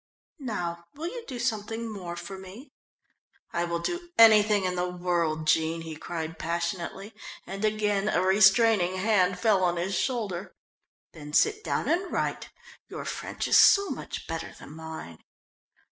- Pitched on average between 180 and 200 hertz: Yes, high, 190 Hz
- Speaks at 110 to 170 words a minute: Yes, average, 155 wpm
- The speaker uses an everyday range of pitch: Yes, average, 4.3 semitones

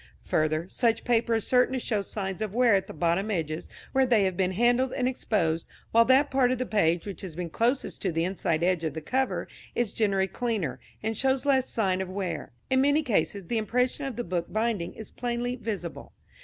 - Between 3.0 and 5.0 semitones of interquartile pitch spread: No, wide, 5.4 semitones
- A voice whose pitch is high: Yes, high, 215 Hz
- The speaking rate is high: Yes, fast, 215 wpm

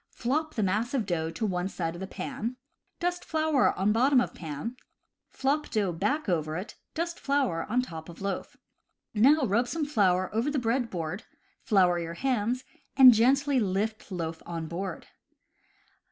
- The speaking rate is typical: Yes, average, 165 wpm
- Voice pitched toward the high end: Yes, high, 215 Hz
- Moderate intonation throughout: No, wide, 6.9 semitones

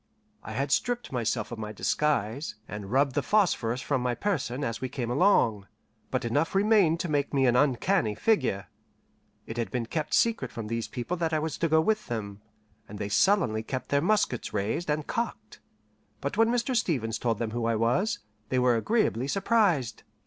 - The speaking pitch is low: Yes, low, 130 Hz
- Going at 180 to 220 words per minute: Yes, average, 190 wpm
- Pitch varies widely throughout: Yes, wide, 7.1 semitones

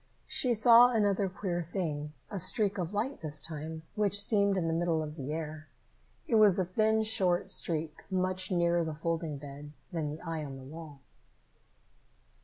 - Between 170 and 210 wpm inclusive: Yes, average, 175 wpm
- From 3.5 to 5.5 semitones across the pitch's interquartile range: Yes, average, 4.4 semitones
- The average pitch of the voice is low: No, medium, 170 Hz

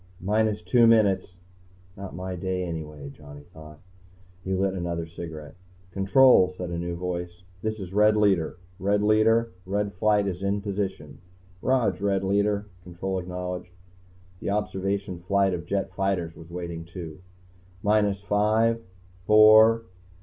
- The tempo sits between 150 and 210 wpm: No, slow, 135 wpm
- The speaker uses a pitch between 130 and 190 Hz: No, very low, 95 Hz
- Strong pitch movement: No, average, 2.9 semitones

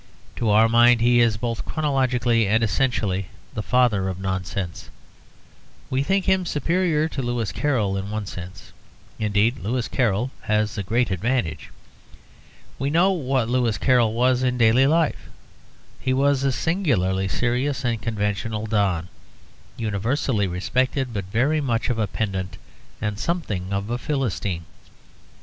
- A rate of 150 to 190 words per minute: No, average, 140 wpm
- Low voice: Yes, low, 115 Hz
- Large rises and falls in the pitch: No, average, 4.3 semitones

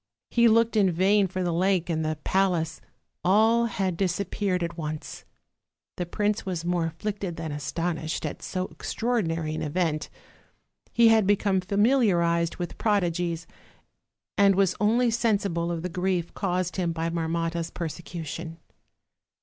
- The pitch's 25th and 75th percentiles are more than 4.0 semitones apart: No, average, 3.2 semitones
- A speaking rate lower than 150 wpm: Yes, average, 140 wpm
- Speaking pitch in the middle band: Yes, medium, 180 Hz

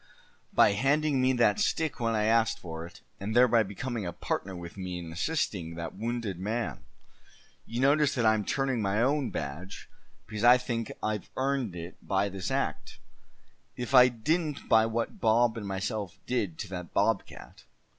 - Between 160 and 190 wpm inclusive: Yes, average, 170 wpm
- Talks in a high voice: No, low, 110 Hz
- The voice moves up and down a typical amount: Yes, average, 4.7 semitones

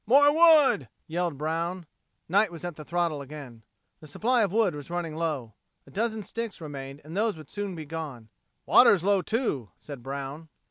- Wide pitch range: Yes, wide, 5.8 semitones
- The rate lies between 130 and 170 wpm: No, average, 180 wpm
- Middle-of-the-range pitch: Yes, medium, 165 Hz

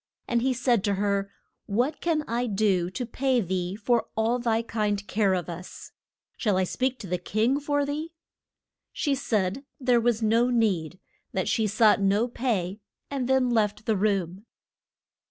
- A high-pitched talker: Yes, high, 220 Hz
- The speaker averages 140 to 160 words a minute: No, average, 170 wpm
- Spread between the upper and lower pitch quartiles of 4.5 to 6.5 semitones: No, average, 3.8 semitones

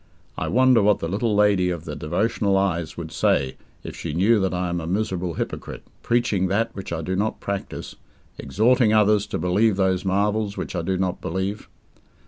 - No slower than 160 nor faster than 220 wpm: Yes, average, 190 wpm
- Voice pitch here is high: No, very low, 95 Hz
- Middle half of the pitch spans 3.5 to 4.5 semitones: No, average, 2.9 semitones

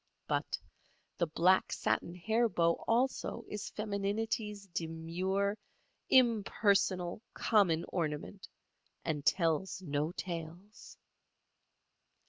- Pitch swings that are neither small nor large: Yes, average, 3.9 semitones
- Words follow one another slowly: Yes, slow, 85 wpm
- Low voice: No, high, 190 Hz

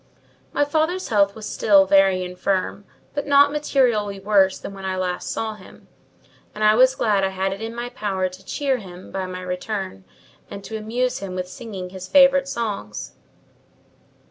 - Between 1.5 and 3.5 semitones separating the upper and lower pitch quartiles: No, average, 4.1 semitones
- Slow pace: No, average, 175 wpm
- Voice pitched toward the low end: No, high, 200 Hz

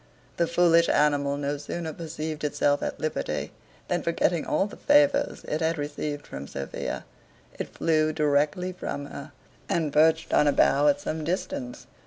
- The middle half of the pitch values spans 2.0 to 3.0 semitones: Yes, narrow, 2.5 semitones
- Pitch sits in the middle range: Yes, medium, 155 Hz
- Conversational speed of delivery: Yes, average, 160 wpm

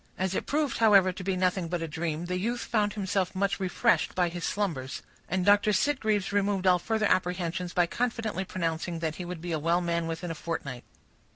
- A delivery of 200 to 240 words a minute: Yes, fast, 205 wpm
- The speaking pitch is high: No, medium, 180 Hz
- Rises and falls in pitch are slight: No, average, 3.2 semitones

